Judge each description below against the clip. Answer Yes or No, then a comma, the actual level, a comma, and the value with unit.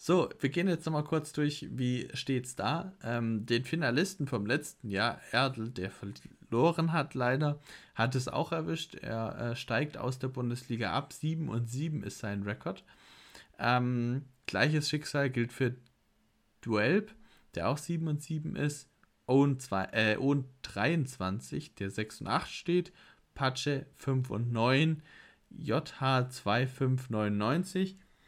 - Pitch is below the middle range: Yes, low, 130 Hz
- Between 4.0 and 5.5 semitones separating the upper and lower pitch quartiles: Yes, average, 4.5 semitones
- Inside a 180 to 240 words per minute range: No, average, 140 wpm